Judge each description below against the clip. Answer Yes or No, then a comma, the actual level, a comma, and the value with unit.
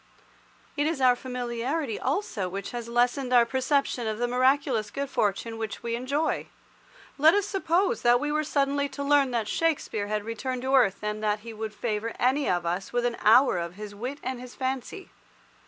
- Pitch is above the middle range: Yes, high, 245 Hz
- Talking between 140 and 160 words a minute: No, average, 190 wpm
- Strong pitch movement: No, average, 4.1 semitones